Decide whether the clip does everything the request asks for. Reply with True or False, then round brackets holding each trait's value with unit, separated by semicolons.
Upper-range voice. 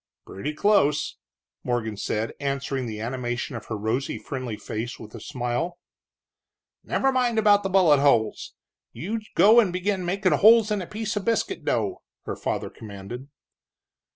False (145 Hz)